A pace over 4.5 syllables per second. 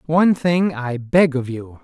No: 4.1 syllables/s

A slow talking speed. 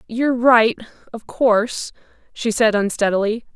Yes: slow, 100 wpm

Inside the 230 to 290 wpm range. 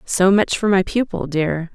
No: fast, 205 wpm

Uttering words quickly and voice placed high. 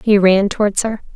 Yes: fast, 210 wpm; high, 205 Hz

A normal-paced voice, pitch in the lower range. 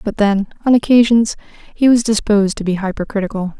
No: average, 185 wpm; high, 210 Hz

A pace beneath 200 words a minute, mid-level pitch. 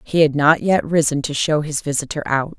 No: fast, 230 wpm; medium, 150 Hz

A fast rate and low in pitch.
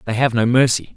Yes: fast, 250 wpm; low, 120 Hz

